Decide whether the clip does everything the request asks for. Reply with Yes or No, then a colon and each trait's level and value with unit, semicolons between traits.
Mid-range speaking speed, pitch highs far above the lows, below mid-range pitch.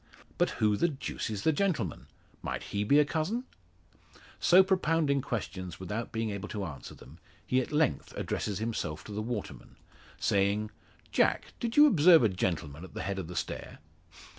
Yes: average, 175 wpm; wide, 8.1 semitones; low, 110 Hz